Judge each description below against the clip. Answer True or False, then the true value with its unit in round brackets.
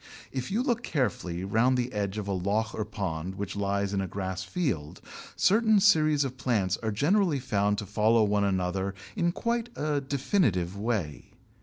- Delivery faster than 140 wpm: True (175 wpm)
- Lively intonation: True (6.7 semitones)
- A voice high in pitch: False (105 Hz)